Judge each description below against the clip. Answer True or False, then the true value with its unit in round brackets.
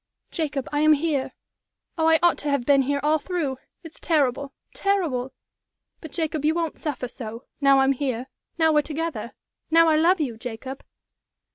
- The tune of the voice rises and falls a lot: False (3.2 semitones)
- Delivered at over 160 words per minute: True (170 wpm)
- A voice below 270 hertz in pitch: False (295 Hz)